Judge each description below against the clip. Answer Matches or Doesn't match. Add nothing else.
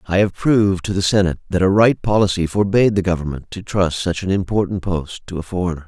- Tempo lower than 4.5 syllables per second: Doesn't match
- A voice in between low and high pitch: Doesn't match